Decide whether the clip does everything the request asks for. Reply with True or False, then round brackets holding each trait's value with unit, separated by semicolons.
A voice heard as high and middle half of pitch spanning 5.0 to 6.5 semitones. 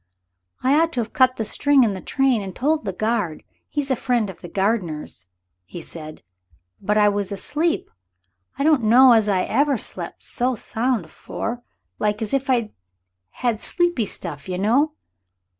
True (225 Hz; 5.3 semitones)